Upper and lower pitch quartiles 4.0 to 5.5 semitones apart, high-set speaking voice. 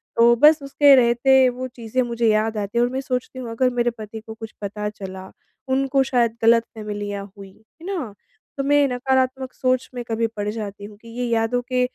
No: average, 3.0 semitones; high, 235 Hz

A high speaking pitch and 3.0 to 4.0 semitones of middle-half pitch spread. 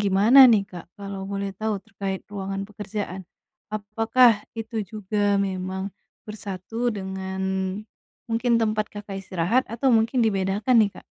No: high, 205 Hz; narrow, 2.6 semitones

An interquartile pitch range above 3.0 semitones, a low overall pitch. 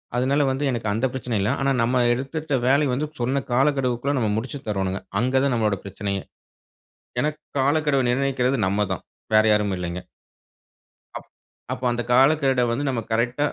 Yes: average, 3.8 semitones; low, 125 Hz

